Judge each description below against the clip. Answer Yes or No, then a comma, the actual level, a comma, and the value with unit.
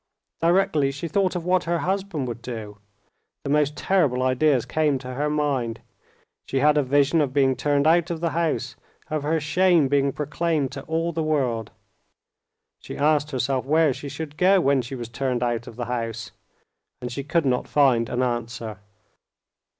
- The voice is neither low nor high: Yes, medium, 145 Hz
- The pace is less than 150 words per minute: No, average, 180 wpm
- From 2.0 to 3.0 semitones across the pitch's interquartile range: No, average, 4.0 semitones